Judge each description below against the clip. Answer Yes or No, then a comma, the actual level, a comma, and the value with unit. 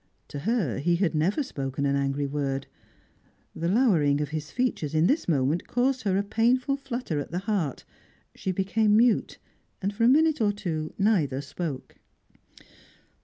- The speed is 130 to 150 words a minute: No, average, 165 wpm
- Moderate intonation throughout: No, wide, 7.5 semitones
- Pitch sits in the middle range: Yes, medium, 180 Hz